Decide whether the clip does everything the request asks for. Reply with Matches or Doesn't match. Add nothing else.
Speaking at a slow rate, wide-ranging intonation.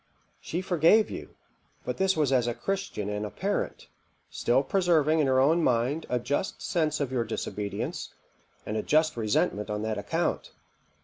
Doesn't match